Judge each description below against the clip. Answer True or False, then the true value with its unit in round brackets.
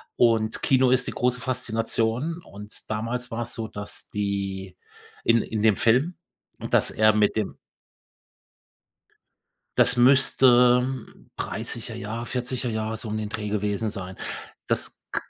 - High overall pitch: False (115 Hz)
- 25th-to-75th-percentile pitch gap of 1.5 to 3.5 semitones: True (2.8 semitones)